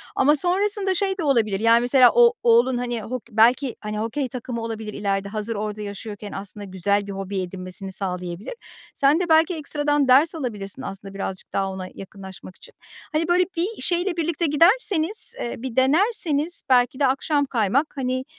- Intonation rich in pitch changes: Yes, wide, 7.4 semitones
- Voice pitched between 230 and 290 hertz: Yes, high, 245 Hz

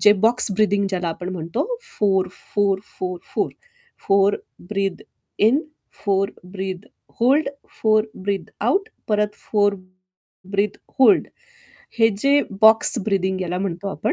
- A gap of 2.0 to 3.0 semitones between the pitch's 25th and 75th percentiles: Yes, narrow, 2.4 semitones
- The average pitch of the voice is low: No, high, 200 Hz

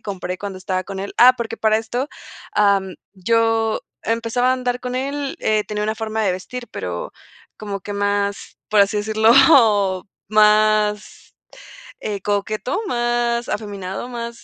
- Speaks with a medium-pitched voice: No, high, 215 Hz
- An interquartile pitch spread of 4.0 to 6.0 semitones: No, average, 2.7 semitones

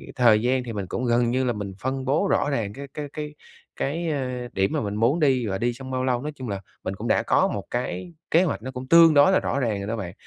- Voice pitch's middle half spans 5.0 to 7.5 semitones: No, average, 4.0 semitones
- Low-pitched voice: Yes, low, 125 Hz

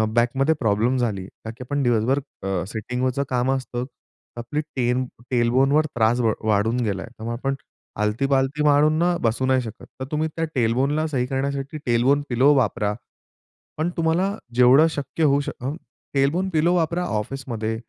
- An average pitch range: Yes, average, 3.4 semitones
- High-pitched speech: No, low, 130 Hz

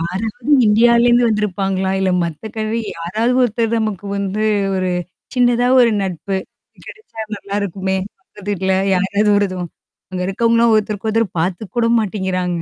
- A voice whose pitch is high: Yes, high, 205 Hz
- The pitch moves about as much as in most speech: Yes, average, 3.2 semitones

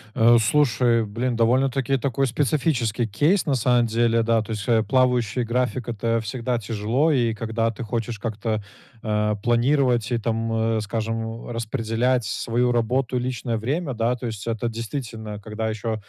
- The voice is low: Yes, low, 115 Hz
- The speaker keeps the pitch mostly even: Yes, narrow, 2.0 semitones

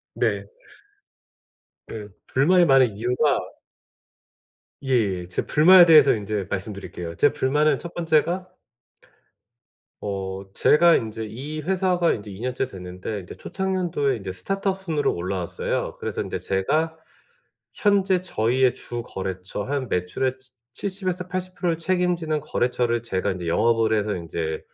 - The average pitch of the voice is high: No, low, 130 Hz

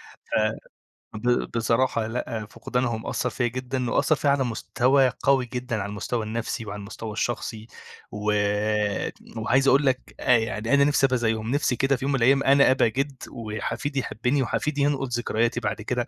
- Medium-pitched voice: No, low, 125 Hz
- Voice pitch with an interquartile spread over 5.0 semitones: No, average, 3.4 semitones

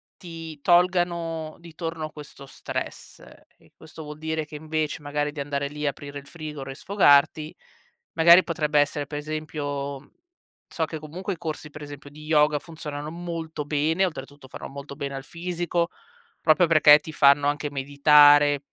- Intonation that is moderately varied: No, narrow, 2.0 semitones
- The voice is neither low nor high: Yes, medium, 150 Hz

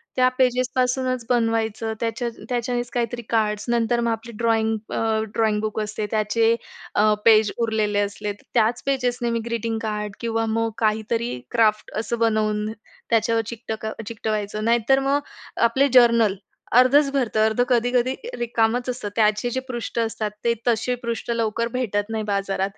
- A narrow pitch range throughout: Yes, narrow, 1.9 semitones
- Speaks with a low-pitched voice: No, high, 230 Hz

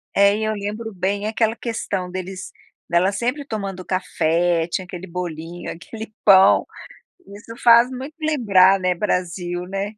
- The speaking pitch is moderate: No, high, 195 Hz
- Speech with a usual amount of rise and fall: Yes, average, 3.4 semitones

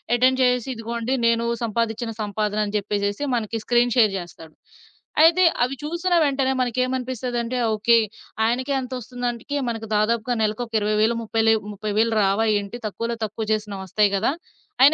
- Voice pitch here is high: Yes, high, 230 Hz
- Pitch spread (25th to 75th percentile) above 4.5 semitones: No, average, 2.8 semitones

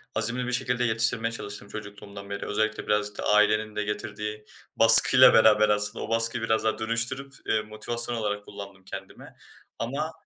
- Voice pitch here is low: Yes, low, 110 Hz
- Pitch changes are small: Yes, narrow, 1.8 semitones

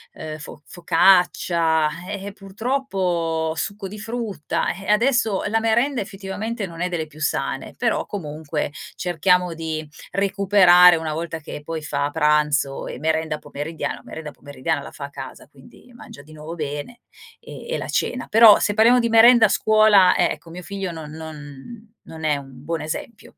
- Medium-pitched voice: Yes, medium, 170 Hz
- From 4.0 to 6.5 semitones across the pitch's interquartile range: Yes, average, 4.9 semitones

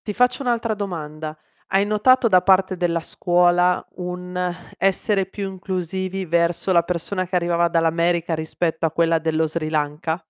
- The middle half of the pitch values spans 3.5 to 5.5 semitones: No, narrow, 2.5 semitones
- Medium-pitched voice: Yes, medium, 175 Hz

